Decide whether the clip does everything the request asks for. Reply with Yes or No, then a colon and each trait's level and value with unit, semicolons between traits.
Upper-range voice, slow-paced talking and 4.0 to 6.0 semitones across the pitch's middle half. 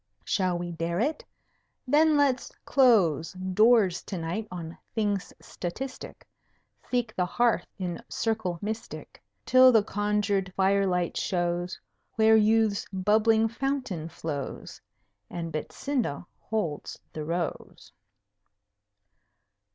Yes: high, 200 Hz; slow, 105 wpm; average, 4.4 semitones